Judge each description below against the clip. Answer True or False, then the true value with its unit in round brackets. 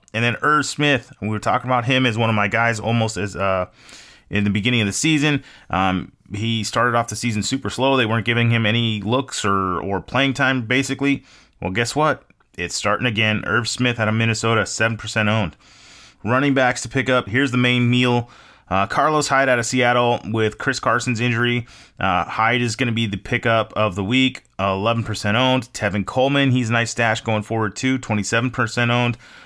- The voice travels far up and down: False (3.0 semitones)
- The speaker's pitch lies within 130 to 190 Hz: False (115 Hz)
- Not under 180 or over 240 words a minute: True (205 wpm)